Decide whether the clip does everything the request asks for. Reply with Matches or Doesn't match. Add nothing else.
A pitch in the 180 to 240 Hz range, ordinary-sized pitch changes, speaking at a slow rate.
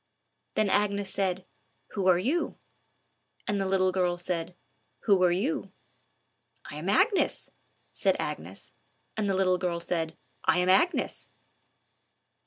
Doesn't match